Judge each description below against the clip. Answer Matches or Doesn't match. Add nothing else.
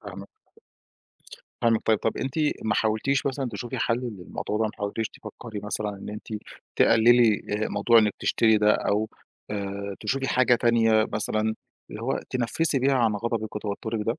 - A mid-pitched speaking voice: Doesn't match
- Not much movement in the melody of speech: Matches